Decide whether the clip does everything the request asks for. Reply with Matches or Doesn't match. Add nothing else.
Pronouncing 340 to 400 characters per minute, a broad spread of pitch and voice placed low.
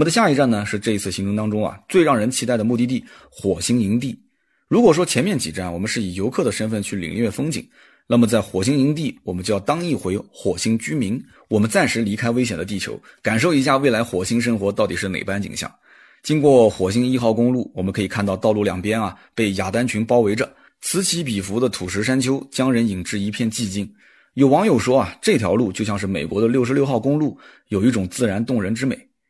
Doesn't match